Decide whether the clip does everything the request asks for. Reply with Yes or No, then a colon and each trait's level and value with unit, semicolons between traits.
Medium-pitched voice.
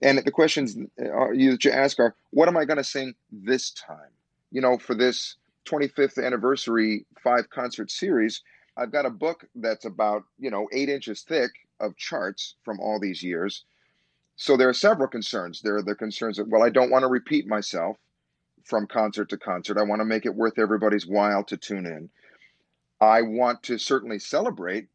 No: low, 115 Hz